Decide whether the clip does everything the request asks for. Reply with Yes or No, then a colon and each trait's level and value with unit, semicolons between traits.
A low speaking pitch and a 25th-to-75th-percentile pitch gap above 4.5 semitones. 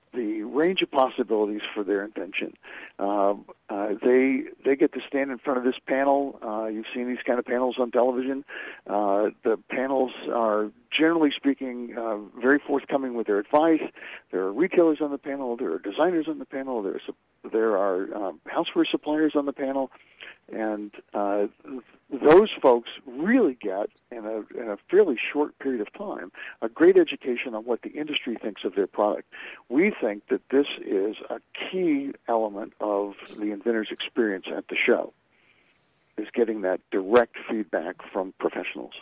Yes: low, 125 Hz; average, 5.1 semitones